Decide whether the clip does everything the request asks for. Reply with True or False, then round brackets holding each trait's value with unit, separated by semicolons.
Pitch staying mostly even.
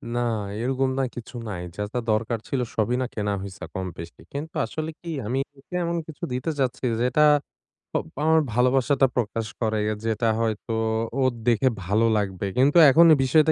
False (4.2 semitones)